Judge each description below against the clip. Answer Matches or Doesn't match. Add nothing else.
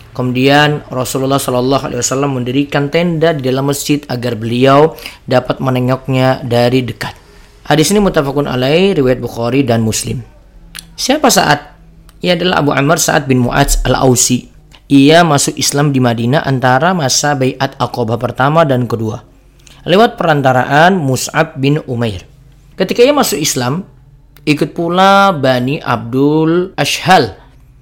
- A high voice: Doesn't match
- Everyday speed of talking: Matches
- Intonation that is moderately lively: Matches